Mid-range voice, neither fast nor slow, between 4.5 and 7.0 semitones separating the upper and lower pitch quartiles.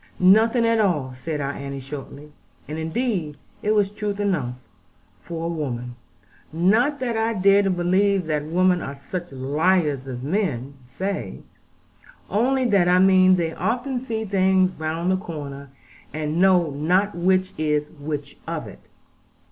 Yes: medium, 175 Hz; average, 150 wpm; average, 5.1 semitones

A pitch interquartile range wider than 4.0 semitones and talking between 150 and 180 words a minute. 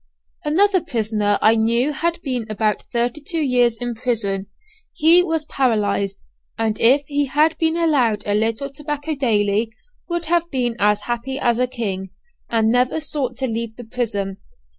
Yes: average, 5.0 semitones; average, 160 wpm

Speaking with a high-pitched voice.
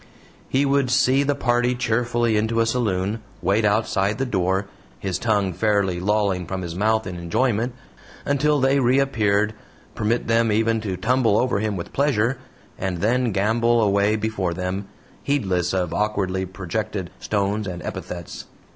No: low, 110 Hz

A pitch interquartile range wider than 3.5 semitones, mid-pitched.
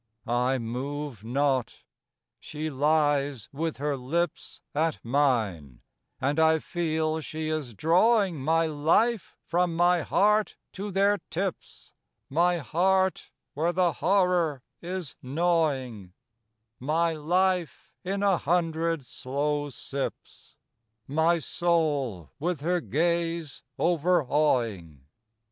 Yes: average, 3.9 semitones; medium, 160 Hz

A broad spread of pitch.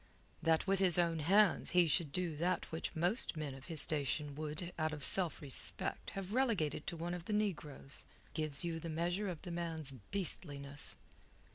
No: average, 3.0 semitones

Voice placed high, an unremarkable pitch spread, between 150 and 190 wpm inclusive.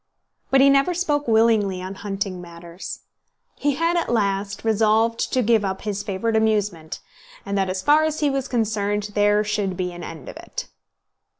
Yes: high, 210 Hz; average, 3.4 semitones; average, 180 wpm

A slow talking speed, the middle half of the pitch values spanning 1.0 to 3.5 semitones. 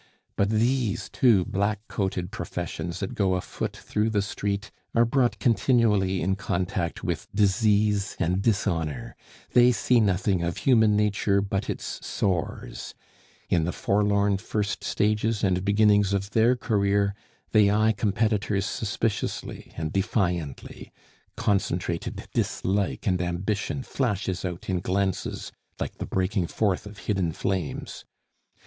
Yes: slow, 130 wpm; narrow, 2.4 semitones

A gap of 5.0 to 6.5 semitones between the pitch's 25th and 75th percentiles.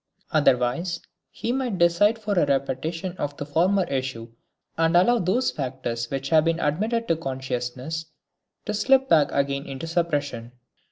Yes: wide, 5.5 semitones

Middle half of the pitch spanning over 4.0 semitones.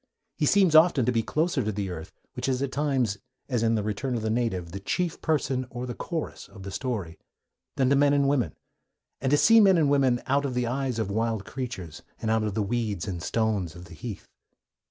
Yes: average, 5.0 semitones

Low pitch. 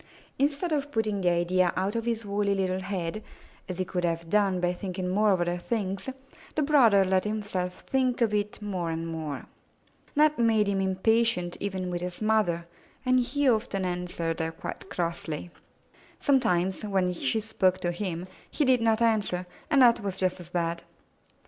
No: high, 195 Hz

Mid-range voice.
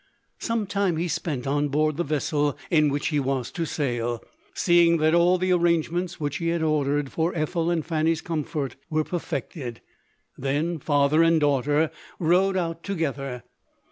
Yes: medium, 155 Hz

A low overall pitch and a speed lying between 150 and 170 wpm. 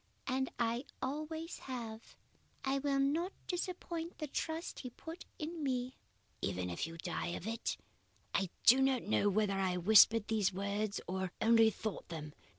No: high, 230 Hz; average, 155 wpm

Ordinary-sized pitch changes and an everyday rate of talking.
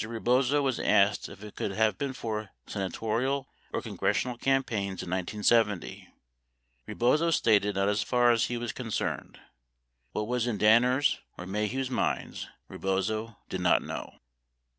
Yes: average, 3.4 semitones; average, 145 wpm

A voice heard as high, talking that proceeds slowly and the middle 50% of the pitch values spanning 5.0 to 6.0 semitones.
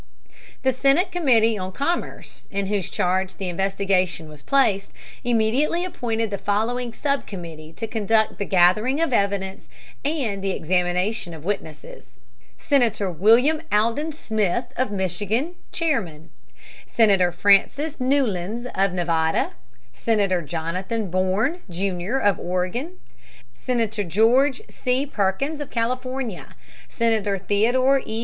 Yes: high, 210 Hz; slow, 120 wpm; wide, 5.4 semitones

